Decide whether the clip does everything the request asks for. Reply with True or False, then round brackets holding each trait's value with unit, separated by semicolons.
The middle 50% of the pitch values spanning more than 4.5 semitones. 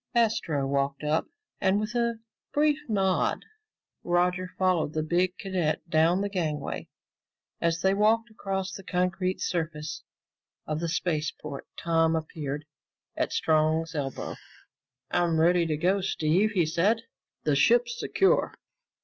False (3.6 semitones)